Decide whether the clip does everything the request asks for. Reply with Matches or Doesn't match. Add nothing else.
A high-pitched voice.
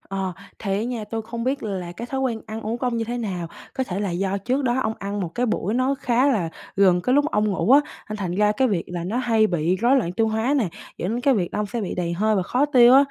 Matches